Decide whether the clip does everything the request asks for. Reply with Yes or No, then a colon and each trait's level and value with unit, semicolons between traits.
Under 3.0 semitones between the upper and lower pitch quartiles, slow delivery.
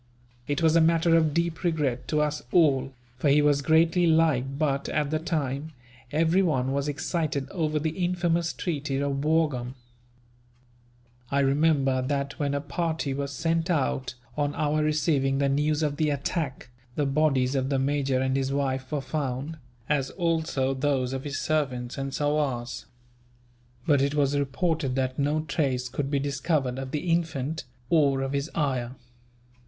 No: narrow, 2.6 semitones; average, 160 wpm